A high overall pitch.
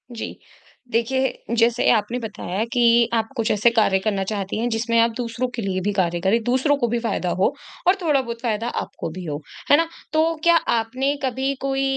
Yes: high, 230 Hz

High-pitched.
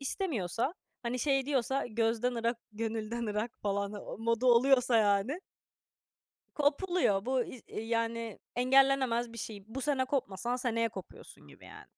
Yes: high, 235 Hz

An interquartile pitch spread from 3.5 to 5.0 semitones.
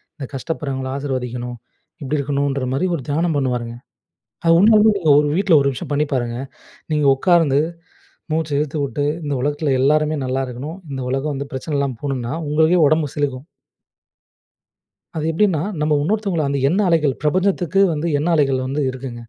No: average, 3.0 semitones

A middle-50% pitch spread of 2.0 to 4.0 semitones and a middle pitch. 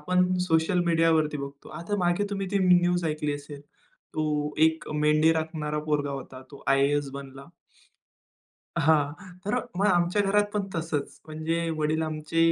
Yes: average, 2.9 semitones; medium, 160 Hz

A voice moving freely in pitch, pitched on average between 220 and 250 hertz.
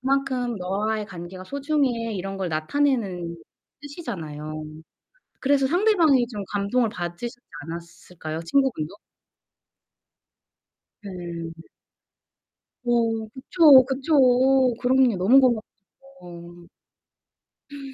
Yes: wide, 7.3 semitones; high, 230 Hz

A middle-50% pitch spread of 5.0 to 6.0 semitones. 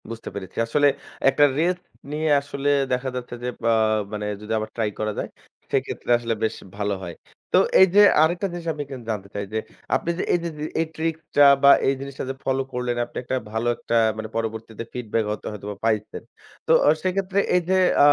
Yes: average, 5.3 semitones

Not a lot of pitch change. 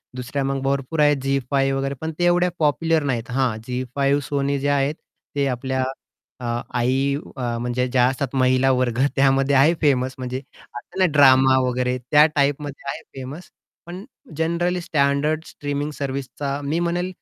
Yes: narrow, 2.2 semitones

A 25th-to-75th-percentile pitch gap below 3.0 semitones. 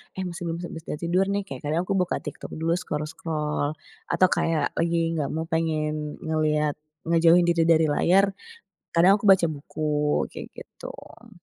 Yes: narrow, 2.5 semitones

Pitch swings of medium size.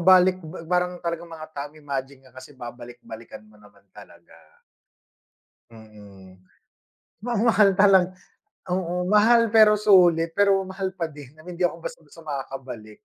No: wide, 6.4 semitones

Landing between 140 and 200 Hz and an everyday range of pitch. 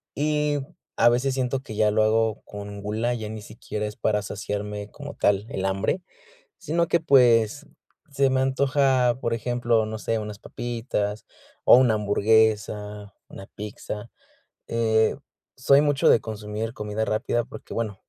No: low, 110 Hz; average, 3.5 semitones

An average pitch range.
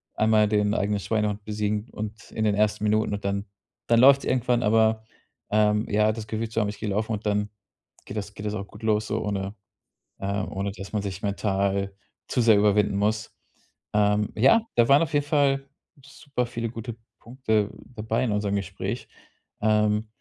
No: narrow, 1.6 semitones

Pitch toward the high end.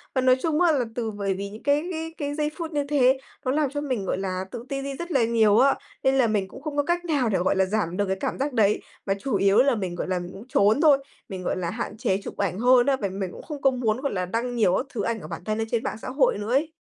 Yes: high, 235 Hz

